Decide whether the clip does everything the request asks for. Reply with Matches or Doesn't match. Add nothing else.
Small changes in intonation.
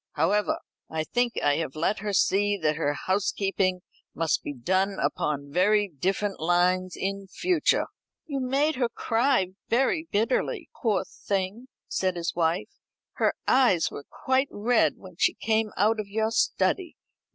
Doesn't match